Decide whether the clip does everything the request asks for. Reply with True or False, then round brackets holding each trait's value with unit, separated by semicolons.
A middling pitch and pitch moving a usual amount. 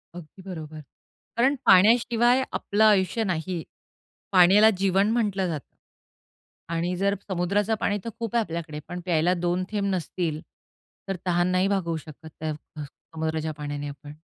True (180 Hz; 4.1 semitones)